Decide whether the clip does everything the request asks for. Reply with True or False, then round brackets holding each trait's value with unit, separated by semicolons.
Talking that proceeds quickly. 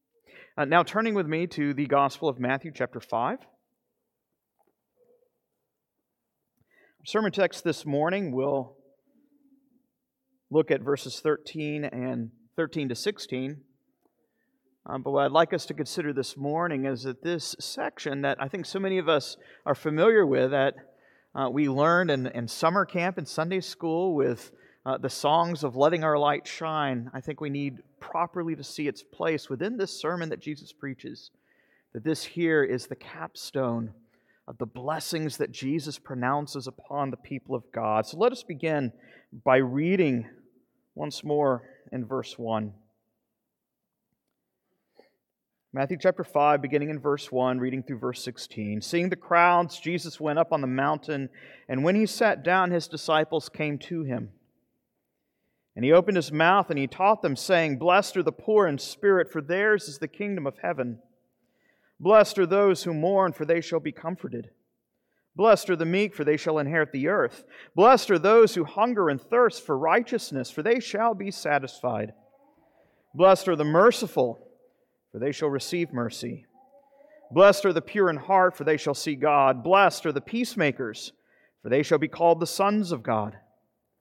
False (165 wpm)